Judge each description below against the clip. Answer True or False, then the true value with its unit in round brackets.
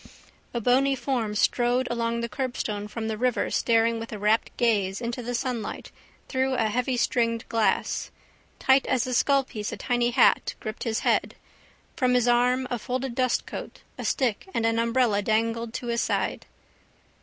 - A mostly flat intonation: True (1.9 semitones)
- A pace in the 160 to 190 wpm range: True (165 wpm)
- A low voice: False (235 Hz)